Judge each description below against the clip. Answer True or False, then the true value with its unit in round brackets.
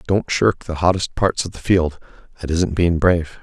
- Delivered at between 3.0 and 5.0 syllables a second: True (4.9 syllables/s)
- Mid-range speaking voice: False (85 Hz)